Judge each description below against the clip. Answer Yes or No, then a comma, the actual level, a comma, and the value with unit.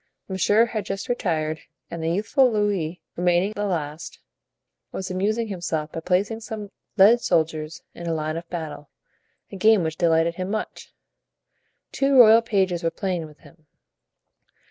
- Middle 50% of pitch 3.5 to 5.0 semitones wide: Yes, average, 4.3 semitones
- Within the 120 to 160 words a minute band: Yes, average, 150 wpm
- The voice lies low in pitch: No, medium, 180 Hz